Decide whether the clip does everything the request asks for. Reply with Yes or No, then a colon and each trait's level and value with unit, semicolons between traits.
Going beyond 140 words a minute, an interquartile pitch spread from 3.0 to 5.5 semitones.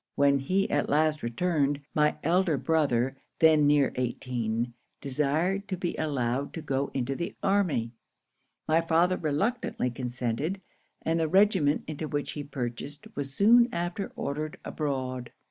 No: slow, 135 wpm; average, 4.0 semitones